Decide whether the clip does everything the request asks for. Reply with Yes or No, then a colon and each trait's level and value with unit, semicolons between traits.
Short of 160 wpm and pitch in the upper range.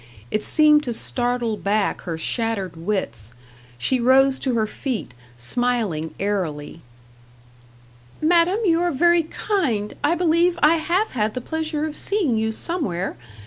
Yes: average, 140 wpm; high, 245 Hz